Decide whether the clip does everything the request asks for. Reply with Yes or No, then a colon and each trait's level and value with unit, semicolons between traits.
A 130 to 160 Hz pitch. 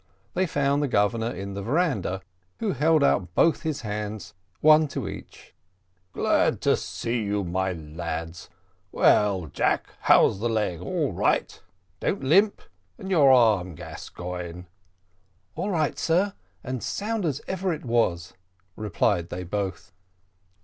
No: low, 110 Hz